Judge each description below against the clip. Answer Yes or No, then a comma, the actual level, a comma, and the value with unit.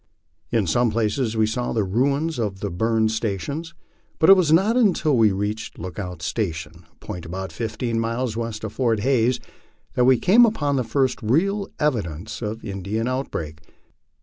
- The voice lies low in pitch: Yes, low, 115 Hz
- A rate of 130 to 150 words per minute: No, average, 175 wpm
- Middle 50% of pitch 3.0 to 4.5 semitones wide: No, average, 4.9 semitones